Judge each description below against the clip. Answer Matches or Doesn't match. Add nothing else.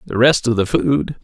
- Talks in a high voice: Doesn't match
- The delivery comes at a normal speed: Doesn't match